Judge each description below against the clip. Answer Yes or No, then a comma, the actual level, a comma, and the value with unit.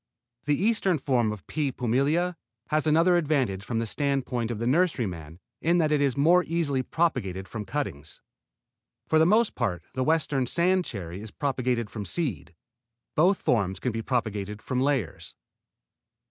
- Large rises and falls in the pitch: Yes, wide, 6.3 semitones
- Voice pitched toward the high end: No, low, 130 Hz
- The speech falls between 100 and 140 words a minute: No, average, 155 wpm